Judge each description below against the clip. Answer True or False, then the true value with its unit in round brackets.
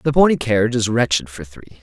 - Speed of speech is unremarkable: False (230 wpm)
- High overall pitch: False (115 Hz)